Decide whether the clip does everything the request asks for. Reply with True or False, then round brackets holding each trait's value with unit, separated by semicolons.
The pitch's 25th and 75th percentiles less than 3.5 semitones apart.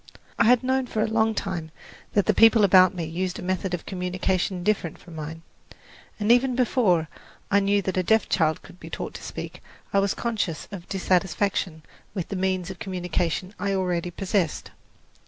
True (2.8 semitones)